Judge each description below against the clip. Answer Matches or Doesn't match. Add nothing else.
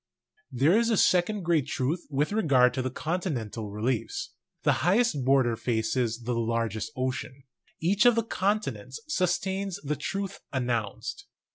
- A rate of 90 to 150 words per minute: Matches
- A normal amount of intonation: Doesn't match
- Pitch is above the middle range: Doesn't match